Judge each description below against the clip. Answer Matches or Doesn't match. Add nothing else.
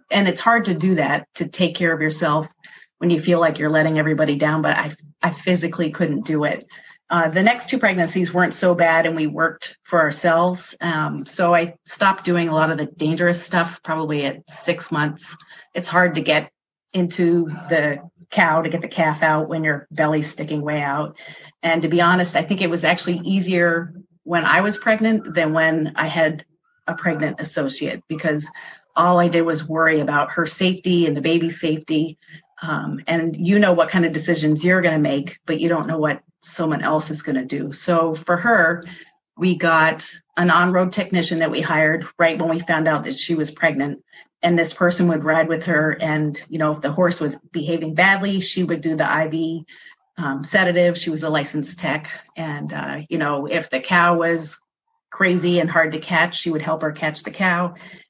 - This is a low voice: Doesn't match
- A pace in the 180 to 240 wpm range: Matches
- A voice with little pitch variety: Matches